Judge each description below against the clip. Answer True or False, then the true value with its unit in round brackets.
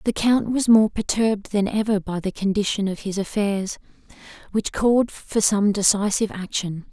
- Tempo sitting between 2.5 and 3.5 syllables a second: False (5.0 syllables/s)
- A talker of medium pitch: False (205 Hz)